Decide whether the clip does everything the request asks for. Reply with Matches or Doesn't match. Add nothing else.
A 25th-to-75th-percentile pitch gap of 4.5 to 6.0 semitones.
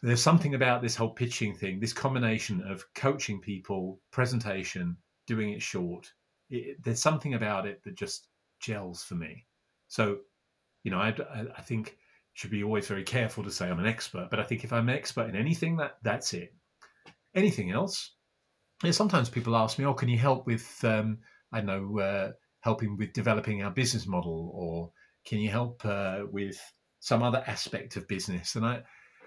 Doesn't match